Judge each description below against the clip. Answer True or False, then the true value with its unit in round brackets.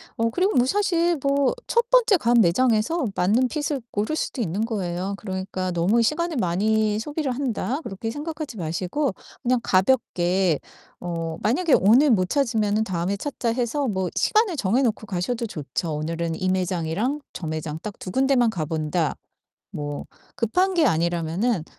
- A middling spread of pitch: False (7.2 semitones)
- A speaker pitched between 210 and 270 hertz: True (220 Hz)